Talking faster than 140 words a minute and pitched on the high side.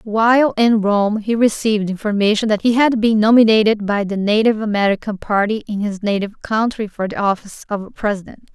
Yes: average, 175 wpm; high, 215 Hz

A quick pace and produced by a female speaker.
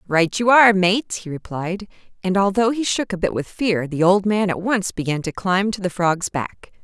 Yes: fast, 230 wpm; female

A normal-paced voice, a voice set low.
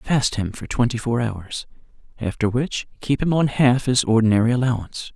Yes: average, 175 wpm; low, 120 Hz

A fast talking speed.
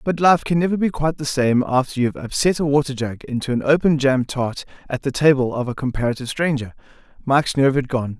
Yes: fast, 225 wpm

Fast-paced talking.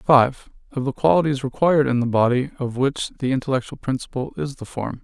No: average, 190 wpm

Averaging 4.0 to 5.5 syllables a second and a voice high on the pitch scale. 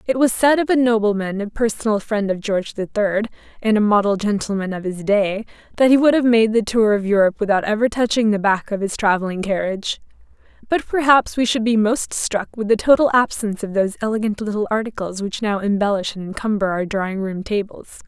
No: 5.8 syllables/s; high, 210 Hz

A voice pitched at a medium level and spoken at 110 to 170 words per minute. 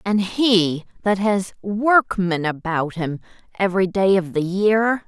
No: high, 195 Hz; average, 140 wpm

